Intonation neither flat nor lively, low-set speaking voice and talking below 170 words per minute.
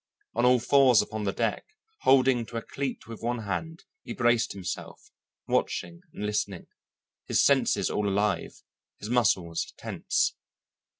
Yes: average, 3.4 semitones; low, 115 Hz; average, 140 wpm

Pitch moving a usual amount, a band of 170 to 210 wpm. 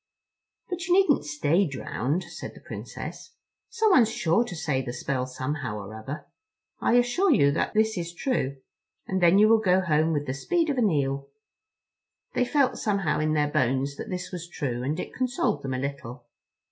No: wide, 8.1 semitones; average, 185 wpm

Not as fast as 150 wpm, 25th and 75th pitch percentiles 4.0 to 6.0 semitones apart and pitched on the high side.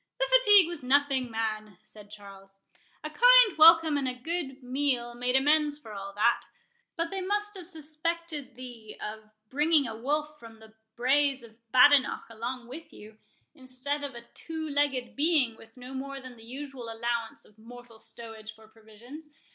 No: average, 170 wpm; average, 4.8 semitones; very high, 255 Hz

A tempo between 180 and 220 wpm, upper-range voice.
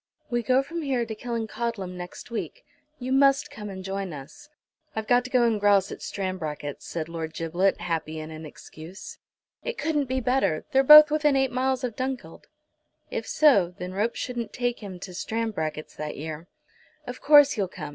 Yes: average, 185 wpm; high, 220 Hz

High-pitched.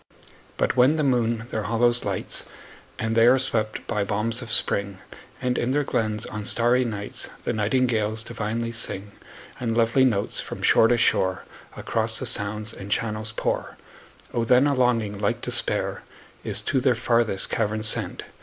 No: low, 115 Hz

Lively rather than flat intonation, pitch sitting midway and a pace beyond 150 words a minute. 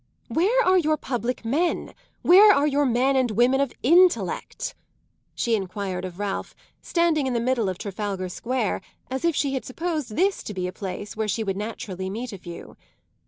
No: wide, 6.9 semitones; high, 245 Hz; average, 185 wpm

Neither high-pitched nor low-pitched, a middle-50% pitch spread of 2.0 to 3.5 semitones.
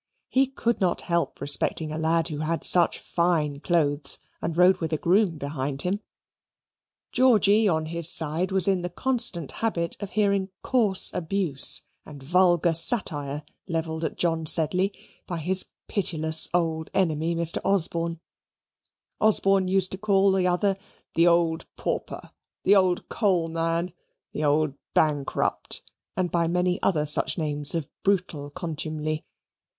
Yes: medium, 170 Hz; average, 3.2 semitones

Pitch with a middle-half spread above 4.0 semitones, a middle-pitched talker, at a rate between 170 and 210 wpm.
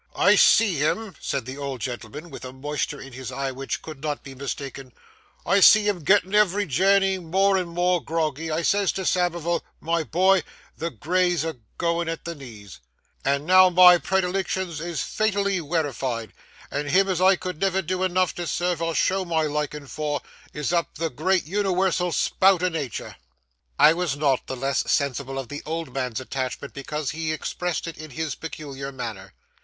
Yes: average, 4.7 semitones; medium, 165 Hz; average, 180 wpm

